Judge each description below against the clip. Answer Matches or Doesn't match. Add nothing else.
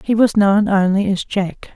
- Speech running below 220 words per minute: Matches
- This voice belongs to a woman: Matches